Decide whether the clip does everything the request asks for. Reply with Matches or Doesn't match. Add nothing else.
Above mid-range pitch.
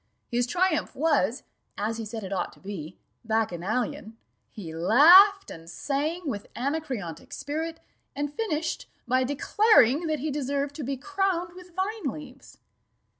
Matches